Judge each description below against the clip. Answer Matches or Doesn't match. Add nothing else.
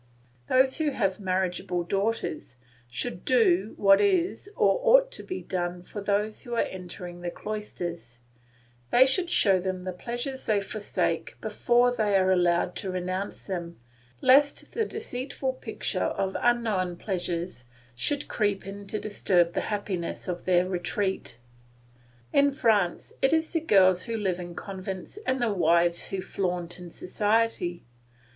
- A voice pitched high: Matches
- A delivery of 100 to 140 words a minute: Doesn't match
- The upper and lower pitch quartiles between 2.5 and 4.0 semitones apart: Doesn't match